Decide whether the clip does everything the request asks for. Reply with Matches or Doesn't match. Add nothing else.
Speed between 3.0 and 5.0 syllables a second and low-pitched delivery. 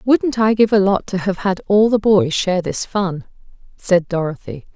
Doesn't match